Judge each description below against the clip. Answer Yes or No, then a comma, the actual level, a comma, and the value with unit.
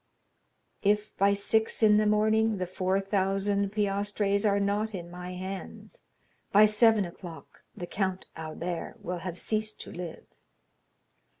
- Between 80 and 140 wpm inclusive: Yes, slow, 135 wpm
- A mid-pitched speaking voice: No, high, 200 Hz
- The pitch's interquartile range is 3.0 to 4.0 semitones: No, narrow, 2.4 semitones